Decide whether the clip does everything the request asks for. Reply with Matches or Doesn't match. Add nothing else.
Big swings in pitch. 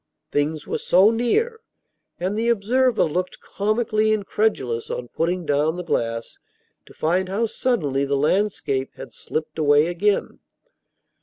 Matches